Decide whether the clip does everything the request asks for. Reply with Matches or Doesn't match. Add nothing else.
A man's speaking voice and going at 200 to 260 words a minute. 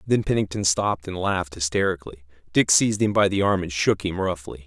Matches